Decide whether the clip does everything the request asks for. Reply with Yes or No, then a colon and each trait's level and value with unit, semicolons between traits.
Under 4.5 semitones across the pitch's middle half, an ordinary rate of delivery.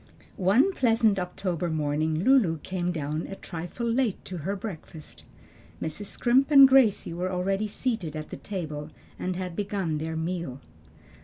No: average, 5.0 semitones; average, 150 wpm